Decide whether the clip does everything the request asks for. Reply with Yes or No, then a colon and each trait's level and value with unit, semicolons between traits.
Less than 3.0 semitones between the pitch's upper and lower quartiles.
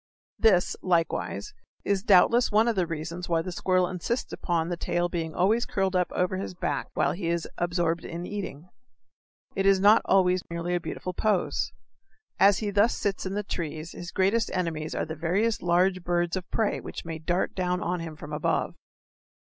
Yes: narrow, 2.4 semitones